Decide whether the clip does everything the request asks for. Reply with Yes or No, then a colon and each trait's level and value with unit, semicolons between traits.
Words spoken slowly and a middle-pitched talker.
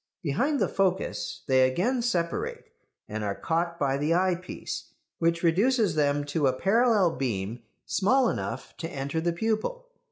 No: average, 150 wpm; medium, 170 Hz